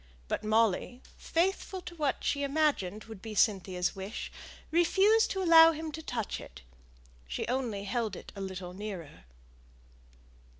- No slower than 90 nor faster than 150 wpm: Yes, average, 140 wpm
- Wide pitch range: Yes, wide, 8.5 semitones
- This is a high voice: Yes, high, 225 Hz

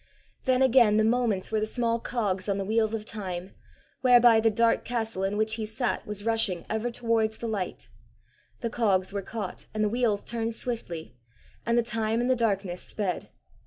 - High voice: Yes, high, 220 Hz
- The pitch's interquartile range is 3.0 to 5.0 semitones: No, narrow, 2.4 semitones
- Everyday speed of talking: Yes, average, 190 wpm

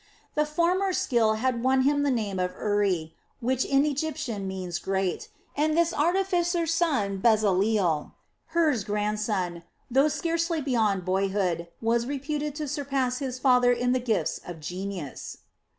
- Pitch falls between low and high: No, high, 245 Hz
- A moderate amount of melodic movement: No, wide, 7.0 semitones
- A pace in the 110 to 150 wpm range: Yes, average, 140 wpm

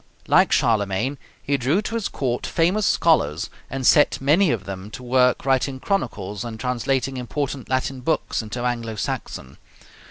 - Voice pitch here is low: Yes, low, 125 Hz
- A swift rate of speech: No, average, 155 wpm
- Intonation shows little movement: No, average, 3.7 semitones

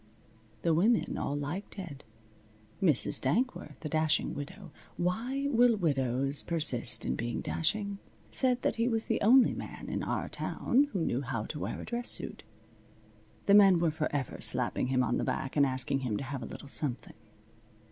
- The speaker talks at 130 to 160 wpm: No, average, 175 wpm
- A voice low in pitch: No, medium, 160 Hz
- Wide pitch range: Yes, wide, 7.4 semitones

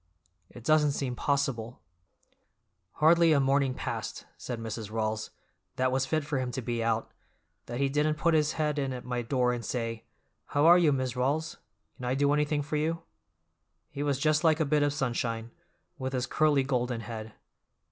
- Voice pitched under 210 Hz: Yes, low, 135 Hz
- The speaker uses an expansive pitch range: No, average, 3.5 semitones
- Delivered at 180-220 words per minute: Yes, average, 185 wpm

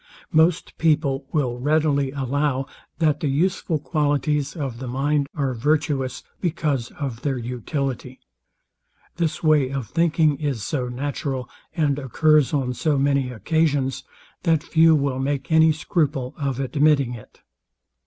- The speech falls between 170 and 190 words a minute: No, slow, 135 wpm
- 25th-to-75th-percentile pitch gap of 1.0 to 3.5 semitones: Yes, average, 2.7 semitones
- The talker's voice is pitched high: No, medium, 140 Hz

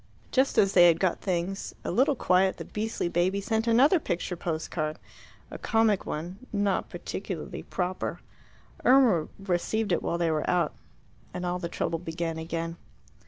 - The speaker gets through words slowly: No, average, 165 wpm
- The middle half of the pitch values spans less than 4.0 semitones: Yes, average, 3.6 semitones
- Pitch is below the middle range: No, medium, 180 Hz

